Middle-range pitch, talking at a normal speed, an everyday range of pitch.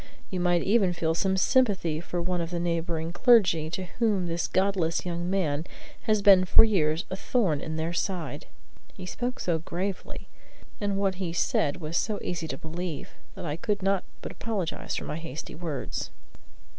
Yes: medium, 175 Hz; average, 180 wpm; average, 3.0 semitones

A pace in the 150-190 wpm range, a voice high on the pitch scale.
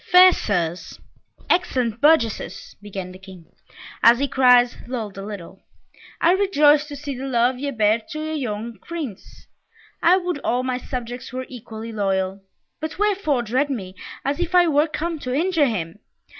Yes: average, 165 wpm; very high, 255 Hz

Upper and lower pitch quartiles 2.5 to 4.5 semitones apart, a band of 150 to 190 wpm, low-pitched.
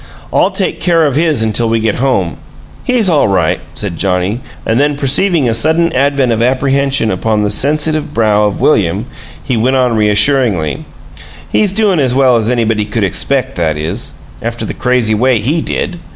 No: average, 5.0 semitones; average, 180 wpm; low, 125 Hz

